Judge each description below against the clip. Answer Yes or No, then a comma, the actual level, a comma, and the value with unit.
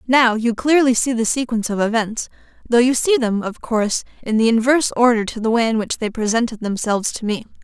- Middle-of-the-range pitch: No, high, 230 Hz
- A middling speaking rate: No, fast, 220 wpm